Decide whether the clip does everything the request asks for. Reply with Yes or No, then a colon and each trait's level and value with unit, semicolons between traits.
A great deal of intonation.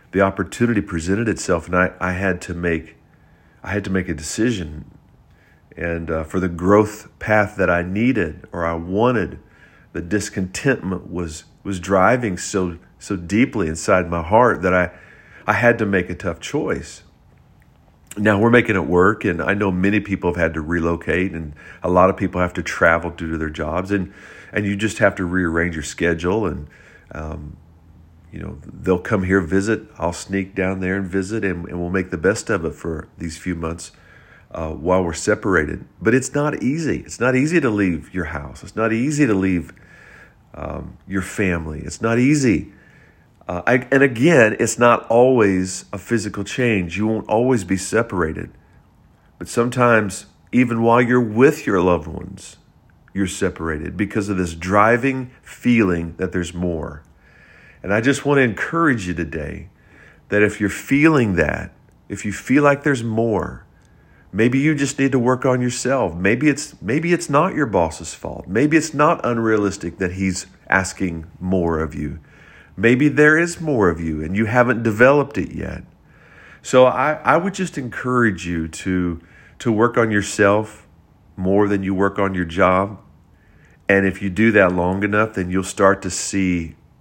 No: average, 4.6 semitones